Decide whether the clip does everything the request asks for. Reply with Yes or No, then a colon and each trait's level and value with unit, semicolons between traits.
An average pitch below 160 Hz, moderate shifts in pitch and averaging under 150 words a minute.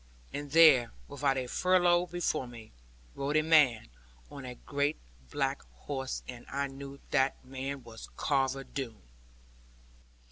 No: medium, 140 Hz; narrow, 2.0 semitones; average, 140 wpm